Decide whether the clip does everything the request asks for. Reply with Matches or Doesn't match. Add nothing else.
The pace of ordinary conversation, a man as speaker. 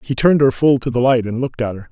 Doesn't match